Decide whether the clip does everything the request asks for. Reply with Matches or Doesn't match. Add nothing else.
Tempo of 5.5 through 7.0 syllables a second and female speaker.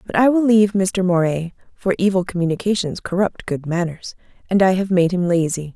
Matches